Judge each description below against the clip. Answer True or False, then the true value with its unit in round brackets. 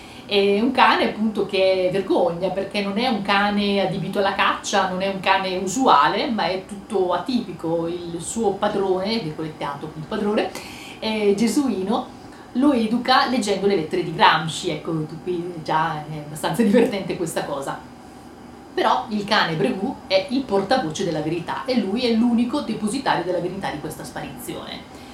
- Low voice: False (195 Hz)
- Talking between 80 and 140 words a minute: False (160 wpm)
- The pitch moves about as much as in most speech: True (4.3 semitones)